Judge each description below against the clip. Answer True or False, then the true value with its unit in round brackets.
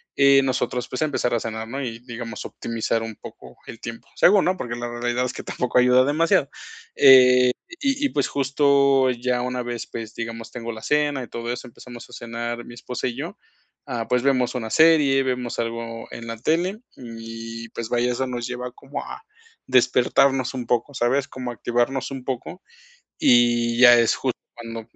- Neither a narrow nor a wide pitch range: False (2.3 semitones)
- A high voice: False (125 Hz)